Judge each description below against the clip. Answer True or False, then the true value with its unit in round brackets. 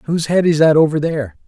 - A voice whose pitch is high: False (155 Hz)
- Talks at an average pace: False (245 wpm)